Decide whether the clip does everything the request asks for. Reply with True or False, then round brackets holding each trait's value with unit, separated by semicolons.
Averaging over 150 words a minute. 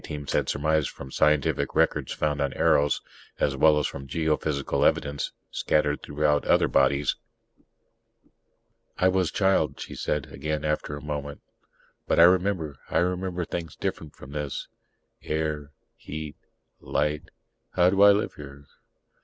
False (145 wpm)